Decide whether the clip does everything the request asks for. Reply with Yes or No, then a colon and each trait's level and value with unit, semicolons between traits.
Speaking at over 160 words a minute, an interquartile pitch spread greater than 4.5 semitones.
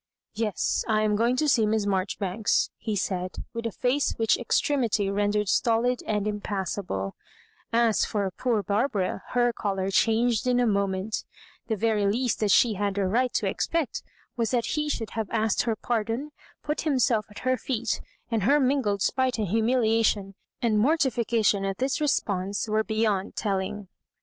No: average, 175 wpm; average, 3.1 semitones